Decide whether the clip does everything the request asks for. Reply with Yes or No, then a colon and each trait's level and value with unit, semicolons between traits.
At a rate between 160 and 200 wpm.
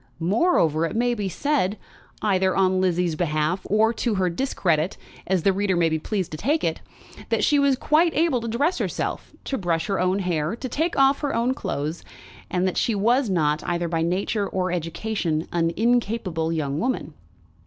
Yes: average, 185 wpm